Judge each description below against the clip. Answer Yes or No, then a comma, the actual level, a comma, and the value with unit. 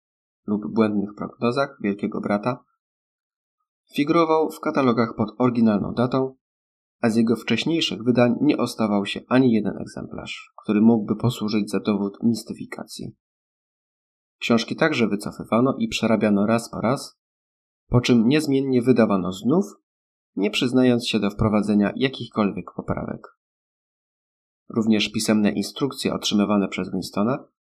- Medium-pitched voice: No, low, 110 Hz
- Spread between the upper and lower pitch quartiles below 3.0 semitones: No, average, 3.5 semitones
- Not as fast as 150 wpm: Yes, average, 115 wpm